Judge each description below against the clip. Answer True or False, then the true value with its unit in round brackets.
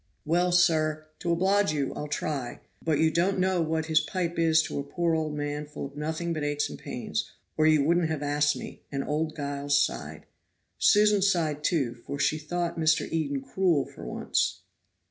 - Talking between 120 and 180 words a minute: False (190 wpm)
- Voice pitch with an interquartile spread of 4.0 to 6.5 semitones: False (2.7 semitones)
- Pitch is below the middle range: False (155 Hz)